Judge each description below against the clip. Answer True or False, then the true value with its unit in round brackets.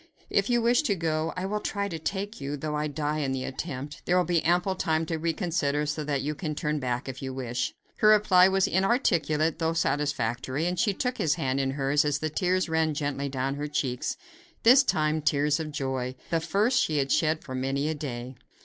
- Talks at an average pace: False (220 wpm)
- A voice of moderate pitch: True (155 Hz)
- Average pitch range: True (4.2 semitones)